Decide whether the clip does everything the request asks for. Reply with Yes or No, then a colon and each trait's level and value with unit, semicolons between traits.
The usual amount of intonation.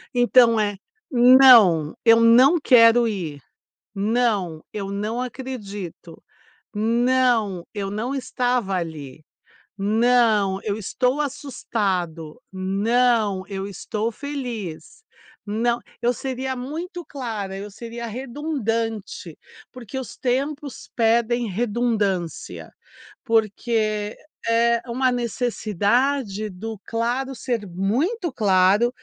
Yes: average, 3.7 semitones